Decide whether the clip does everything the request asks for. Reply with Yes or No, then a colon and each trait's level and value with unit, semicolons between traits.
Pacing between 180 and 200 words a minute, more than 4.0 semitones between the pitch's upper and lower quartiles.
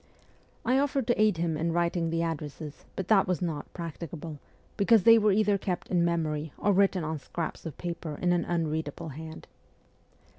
No: average, 185 wpm; average, 3.3 semitones